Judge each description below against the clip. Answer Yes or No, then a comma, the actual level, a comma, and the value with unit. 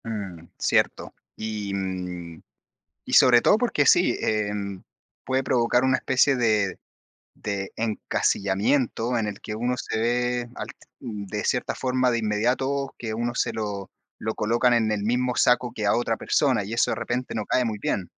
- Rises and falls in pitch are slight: No, average, 3.2 semitones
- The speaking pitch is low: Yes, low, 115 Hz